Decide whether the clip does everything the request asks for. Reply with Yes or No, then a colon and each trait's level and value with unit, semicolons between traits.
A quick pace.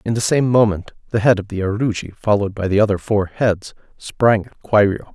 Yes: fast, 210 wpm